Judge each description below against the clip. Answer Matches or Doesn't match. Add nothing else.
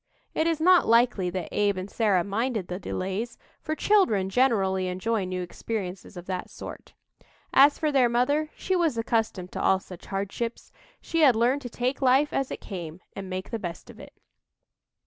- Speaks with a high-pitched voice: Matches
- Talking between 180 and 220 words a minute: Matches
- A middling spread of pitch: Doesn't match